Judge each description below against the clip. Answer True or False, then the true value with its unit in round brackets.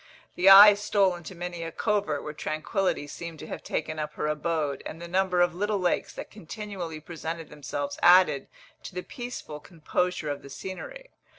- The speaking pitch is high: False (175 Hz)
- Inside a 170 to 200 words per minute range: True (180 wpm)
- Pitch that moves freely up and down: False (3.9 semitones)